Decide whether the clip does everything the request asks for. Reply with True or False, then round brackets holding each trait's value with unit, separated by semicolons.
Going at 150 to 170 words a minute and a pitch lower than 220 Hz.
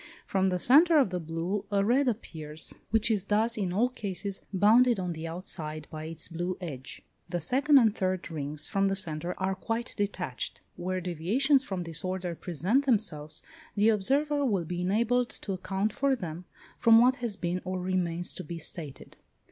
False (180 wpm; 190 Hz)